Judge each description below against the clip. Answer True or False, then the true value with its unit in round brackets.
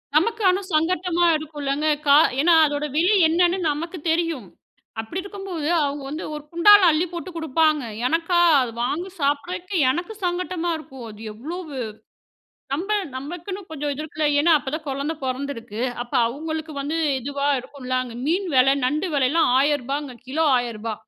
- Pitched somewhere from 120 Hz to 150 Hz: False (310 Hz)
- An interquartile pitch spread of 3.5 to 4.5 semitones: True (3.8 semitones)